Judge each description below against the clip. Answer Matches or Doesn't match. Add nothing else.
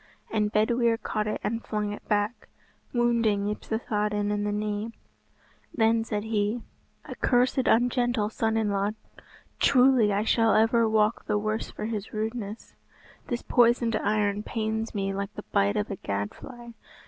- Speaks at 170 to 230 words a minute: Doesn't match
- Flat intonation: Matches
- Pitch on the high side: Matches